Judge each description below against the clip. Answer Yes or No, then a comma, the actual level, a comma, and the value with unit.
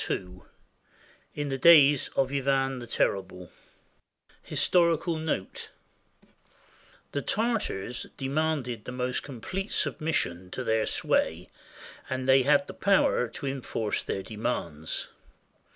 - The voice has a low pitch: Yes, low, 130 Hz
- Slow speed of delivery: Yes, slow, 110 wpm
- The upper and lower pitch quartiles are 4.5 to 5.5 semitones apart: Yes, average, 5.1 semitones